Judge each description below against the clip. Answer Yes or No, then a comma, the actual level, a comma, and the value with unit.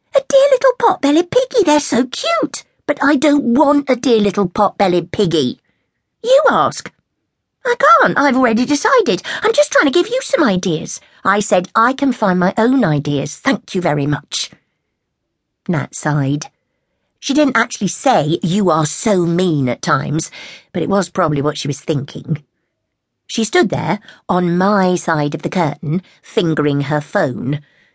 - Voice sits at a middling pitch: No, high, 200 Hz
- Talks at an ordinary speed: Yes, average, 160 wpm